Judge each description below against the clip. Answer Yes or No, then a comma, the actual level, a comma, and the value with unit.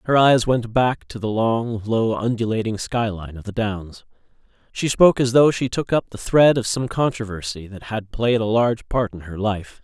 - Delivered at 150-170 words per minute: No, fast, 205 wpm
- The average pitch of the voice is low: Yes, low, 110 Hz